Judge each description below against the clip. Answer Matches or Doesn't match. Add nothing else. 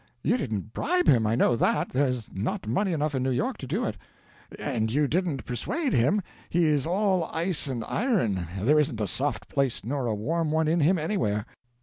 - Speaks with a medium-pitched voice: Matches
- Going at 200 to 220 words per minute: Matches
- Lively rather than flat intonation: Matches